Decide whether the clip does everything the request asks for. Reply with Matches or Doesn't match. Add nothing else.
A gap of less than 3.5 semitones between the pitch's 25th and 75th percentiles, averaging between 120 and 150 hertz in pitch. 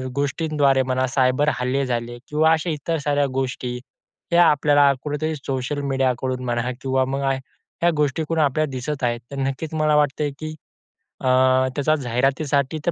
Matches